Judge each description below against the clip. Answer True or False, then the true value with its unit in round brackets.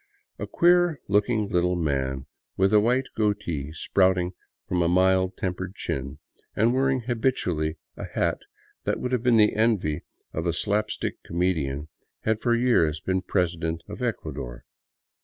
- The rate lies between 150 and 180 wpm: True (155 wpm)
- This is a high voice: False (95 Hz)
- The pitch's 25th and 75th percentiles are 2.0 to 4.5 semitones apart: False (5.2 semitones)